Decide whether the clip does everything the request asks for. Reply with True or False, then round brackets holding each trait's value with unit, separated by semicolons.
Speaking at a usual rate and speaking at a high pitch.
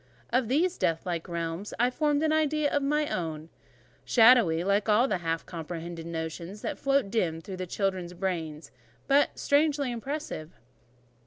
True (150 wpm; 200 Hz)